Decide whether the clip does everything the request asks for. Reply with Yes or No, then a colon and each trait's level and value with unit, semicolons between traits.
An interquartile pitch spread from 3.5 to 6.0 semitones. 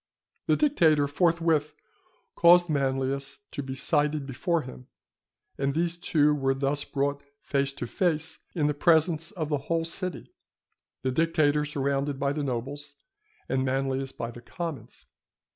No: average, 3.1 semitones